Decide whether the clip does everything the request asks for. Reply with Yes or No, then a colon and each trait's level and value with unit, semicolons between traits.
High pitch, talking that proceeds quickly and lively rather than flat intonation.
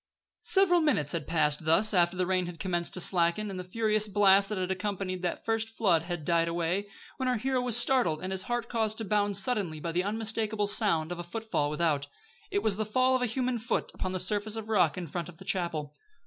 No: high, 195 Hz; fast, 230 wpm; average, 4.4 semitones